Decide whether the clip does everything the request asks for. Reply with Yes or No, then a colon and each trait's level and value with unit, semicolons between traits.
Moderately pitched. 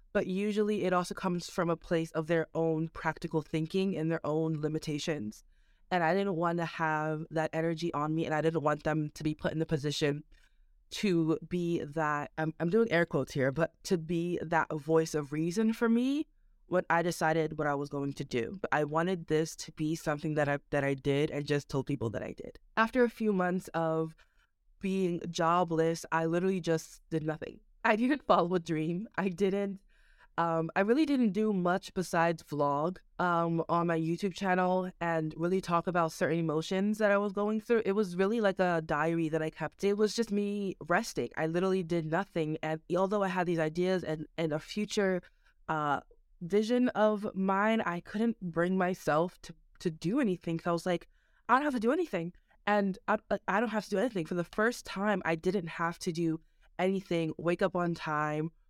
Yes: medium, 170 Hz